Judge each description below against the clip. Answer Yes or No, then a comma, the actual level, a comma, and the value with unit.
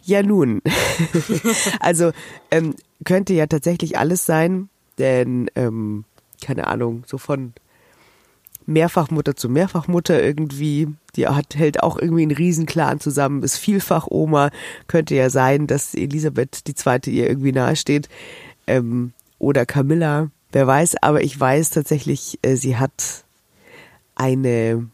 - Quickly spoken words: No, average, 130 wpm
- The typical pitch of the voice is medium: Yes, medium, 150 Hz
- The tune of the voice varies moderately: Yes, average, 4.1 semitones